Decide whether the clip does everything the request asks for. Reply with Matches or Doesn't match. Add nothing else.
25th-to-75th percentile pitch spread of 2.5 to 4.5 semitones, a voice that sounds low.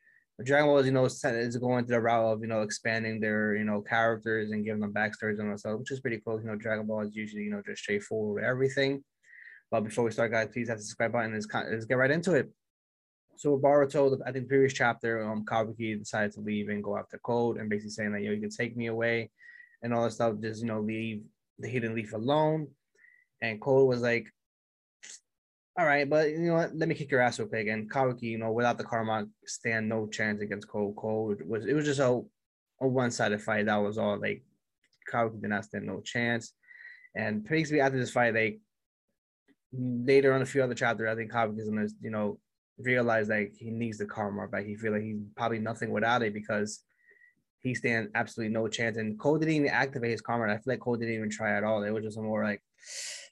Matches